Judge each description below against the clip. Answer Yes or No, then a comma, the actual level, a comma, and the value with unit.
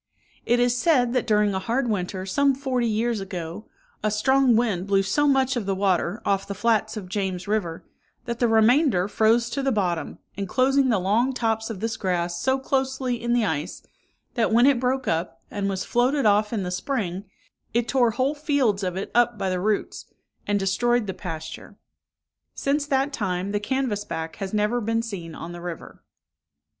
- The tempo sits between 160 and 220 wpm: Yes, average, 190 wpm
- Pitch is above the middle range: Yes, high, 220 Hz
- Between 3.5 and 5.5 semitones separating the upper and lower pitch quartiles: Yes, average, 4.4 semitones